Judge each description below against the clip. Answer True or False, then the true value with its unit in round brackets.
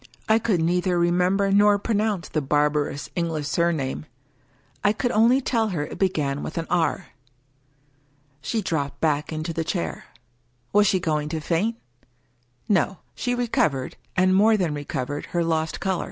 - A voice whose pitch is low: False (170 Hz)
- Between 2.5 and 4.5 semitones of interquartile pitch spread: False (5.1 semitones)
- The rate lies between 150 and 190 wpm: True (155 wpm)